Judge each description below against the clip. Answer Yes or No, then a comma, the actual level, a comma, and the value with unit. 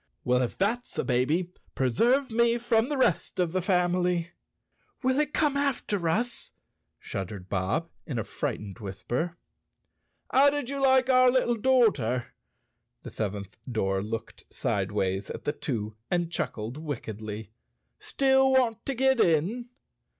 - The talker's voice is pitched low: No, medium, 175 Hz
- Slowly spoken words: No, average, 145 wpm